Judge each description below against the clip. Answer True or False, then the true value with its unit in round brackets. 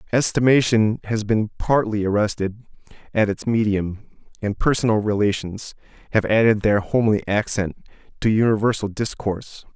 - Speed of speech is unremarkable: False (115 wpm)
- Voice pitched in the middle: False (105 Hz)